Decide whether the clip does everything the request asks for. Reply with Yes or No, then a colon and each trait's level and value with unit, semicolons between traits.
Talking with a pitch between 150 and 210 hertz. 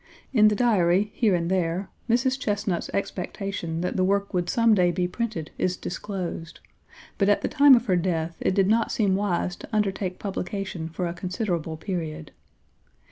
Yes: high, 190 Hz